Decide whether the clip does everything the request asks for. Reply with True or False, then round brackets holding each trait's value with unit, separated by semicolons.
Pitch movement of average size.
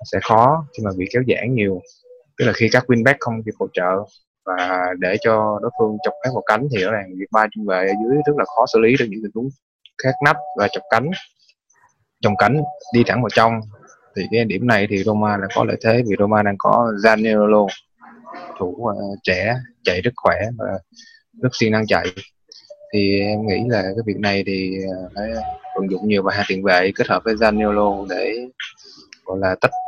True (3.9 semitones)